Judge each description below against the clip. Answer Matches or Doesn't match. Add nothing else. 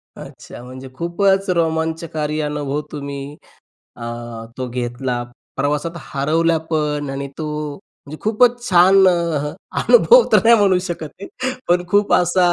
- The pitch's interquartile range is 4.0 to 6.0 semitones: Matches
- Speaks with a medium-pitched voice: Matches